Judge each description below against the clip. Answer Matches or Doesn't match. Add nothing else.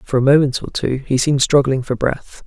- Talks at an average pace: Doesn't match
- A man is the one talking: Matches